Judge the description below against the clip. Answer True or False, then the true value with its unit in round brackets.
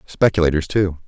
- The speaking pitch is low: True (85 Hz)